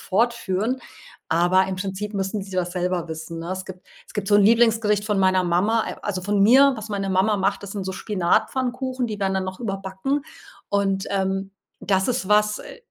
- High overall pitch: Yes, high, 195 Hz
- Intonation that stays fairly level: Yes, narrow, 2.3 semitones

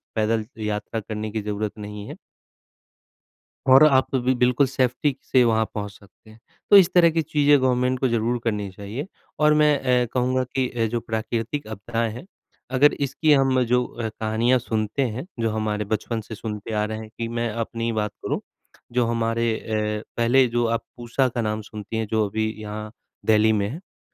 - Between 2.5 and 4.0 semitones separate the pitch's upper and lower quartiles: Yes, average, 2.9 semitones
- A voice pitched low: Yes, low, 115 Hz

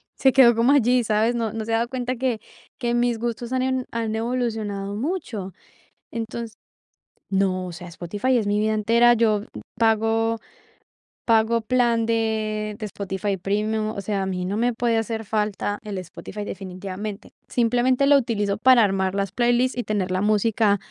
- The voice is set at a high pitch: Yes, high, 220 Hz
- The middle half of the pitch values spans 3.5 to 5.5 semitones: No, average, 2.7 semitones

